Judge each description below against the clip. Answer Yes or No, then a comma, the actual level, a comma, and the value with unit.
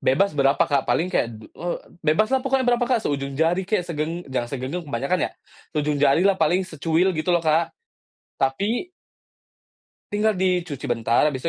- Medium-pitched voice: Yes, medium, 165 Hz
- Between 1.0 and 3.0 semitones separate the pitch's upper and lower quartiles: No, average, 5.0 semitones